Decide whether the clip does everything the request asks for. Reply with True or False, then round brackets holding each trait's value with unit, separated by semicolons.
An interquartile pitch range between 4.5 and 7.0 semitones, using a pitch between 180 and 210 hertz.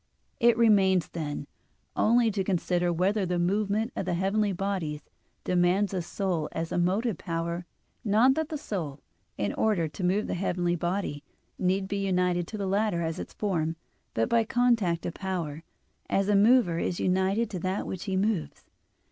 False (3.2 semitones; 190 Hz)